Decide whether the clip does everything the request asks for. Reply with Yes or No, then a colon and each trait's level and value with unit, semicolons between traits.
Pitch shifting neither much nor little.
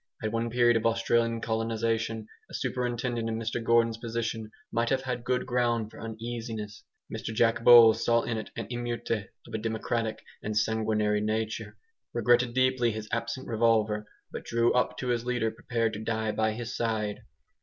No: narrow, 1.3 semitones